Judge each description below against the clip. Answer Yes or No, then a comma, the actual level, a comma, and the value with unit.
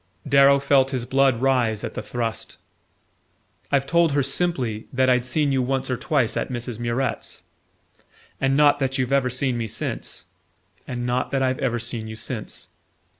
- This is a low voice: Yes, low, 130 Hz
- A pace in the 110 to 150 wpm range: No, average, 175 wpm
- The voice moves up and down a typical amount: No, narrow, 2.3 semitones